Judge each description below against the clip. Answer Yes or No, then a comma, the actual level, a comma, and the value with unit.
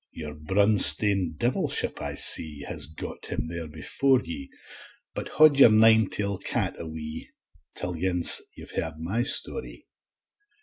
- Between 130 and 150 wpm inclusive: Yes, average, 140 wpm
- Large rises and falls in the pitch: Yes, wide, 5.7 semitones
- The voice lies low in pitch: Yes, very low, 90 Hz